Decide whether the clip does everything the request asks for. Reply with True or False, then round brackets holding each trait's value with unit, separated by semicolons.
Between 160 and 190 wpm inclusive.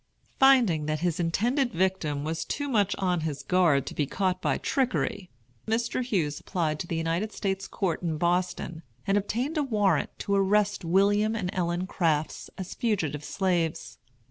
True (165 wpm)